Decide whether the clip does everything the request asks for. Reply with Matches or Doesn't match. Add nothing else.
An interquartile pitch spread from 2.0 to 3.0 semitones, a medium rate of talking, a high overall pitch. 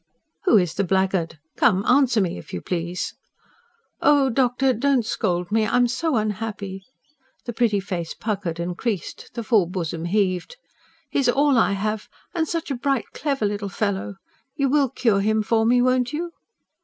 Doesn't match